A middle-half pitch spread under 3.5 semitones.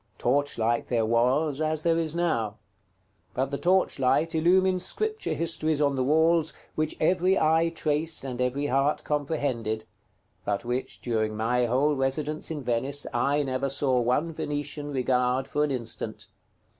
No: average, 3.9 semitones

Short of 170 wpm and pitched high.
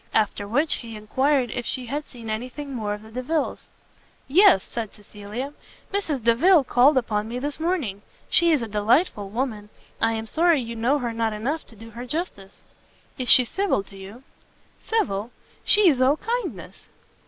No: average, 175 wpm; high, 245 Hz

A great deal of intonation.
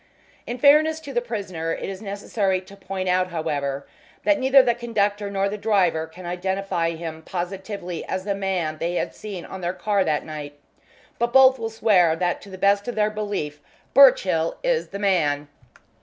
No: average, 3.9 semitones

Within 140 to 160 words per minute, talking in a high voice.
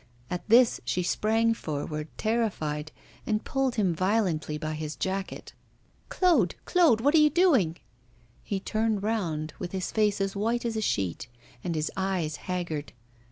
Yes: average, 155 wpm; high, 195 Hz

